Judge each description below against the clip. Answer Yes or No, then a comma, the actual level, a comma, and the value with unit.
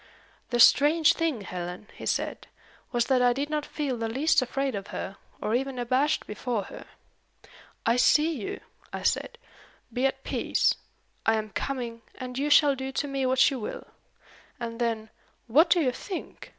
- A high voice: Yes, very high, 255 Hz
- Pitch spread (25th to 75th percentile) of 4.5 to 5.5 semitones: No, average, 3.7 semitones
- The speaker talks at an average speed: Yes, average, 175 wpm